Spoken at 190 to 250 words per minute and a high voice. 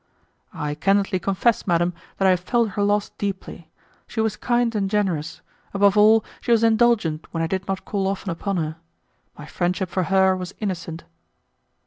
No: average, 175 wpm; high, 195 Hz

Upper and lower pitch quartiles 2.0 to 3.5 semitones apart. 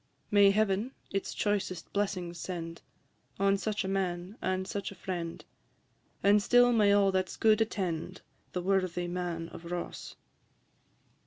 Yes: narrow, 2.4 semitones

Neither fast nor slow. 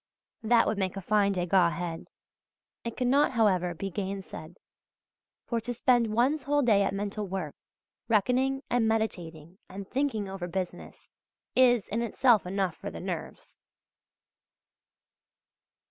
No: slow, 130 wpm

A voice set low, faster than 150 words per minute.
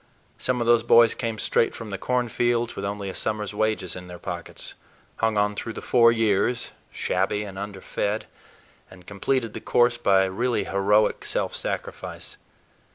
Yes: low, 105 Hz; average, 160 wpm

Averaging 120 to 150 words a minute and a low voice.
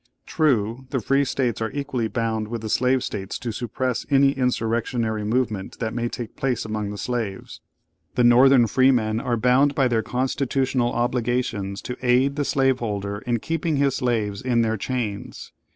No: average, 165 wpm; low, 120 Hz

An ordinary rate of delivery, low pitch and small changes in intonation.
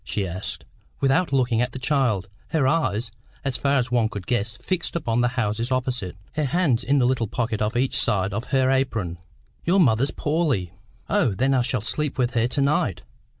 No: average, 195 wpm; low, 125 Hz; average, 3.6 semitones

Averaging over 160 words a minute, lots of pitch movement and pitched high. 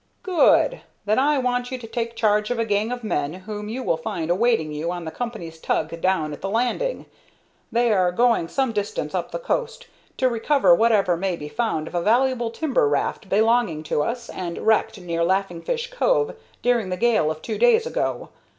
Yes: average, 200 wpm; wide, 5.9 semitones; high, 220 Hz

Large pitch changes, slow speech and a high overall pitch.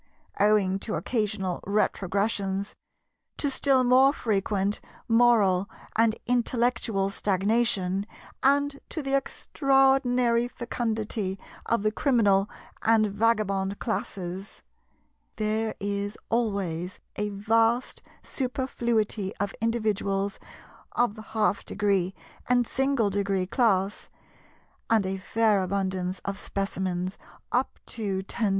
No: average, 3.2 semitones; slow, 100 wpm; high, 210 Hz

